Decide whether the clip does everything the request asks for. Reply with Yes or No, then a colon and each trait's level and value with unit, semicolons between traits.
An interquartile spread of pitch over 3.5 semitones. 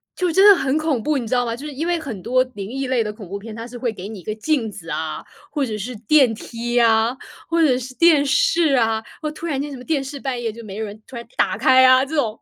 Yes: average, 4.5 semitones